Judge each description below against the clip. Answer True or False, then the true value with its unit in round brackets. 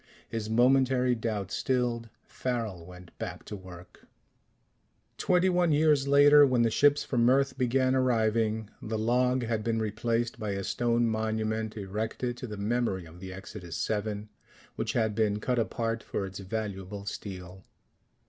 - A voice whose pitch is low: True (110 Hz)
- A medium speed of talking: True (150 wpm)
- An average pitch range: True (3.3 semitones)